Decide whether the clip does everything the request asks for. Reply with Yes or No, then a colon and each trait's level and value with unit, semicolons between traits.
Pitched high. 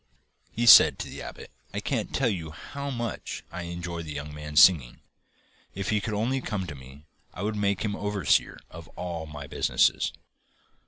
No: very low, 90 Hz